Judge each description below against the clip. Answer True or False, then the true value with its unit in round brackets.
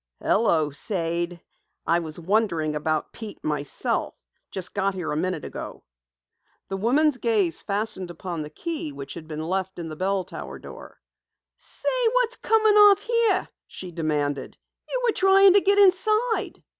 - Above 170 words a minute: False (155 wpm)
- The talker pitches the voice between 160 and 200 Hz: True (190 Hz)